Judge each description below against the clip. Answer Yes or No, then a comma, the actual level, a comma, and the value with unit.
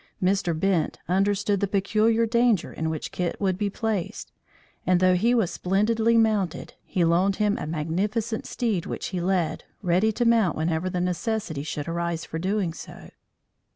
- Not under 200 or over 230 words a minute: No, average, 165 wpm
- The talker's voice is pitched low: No, high, 190 Hz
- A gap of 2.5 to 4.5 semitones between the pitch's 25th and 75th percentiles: Yes, average, 4.0 semitones